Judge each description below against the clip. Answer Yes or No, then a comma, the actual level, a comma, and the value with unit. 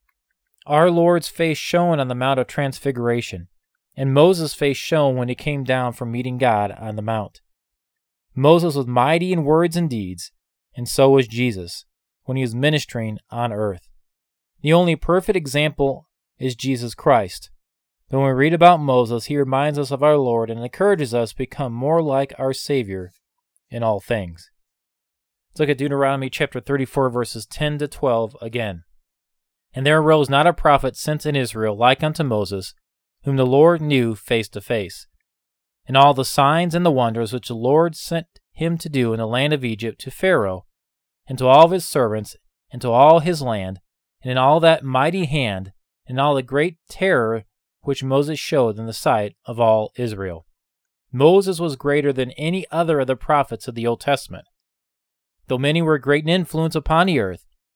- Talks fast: No, average, 180 wpm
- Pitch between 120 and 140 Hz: Yes, low, 135 Hz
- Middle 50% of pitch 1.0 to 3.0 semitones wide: No, average, 4.8 semitones